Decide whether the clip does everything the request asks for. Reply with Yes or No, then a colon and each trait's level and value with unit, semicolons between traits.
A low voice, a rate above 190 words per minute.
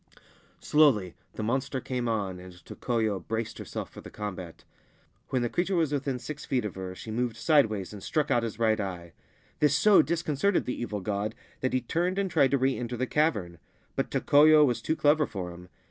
Yes: low, 120 Hz; average, 200 wpm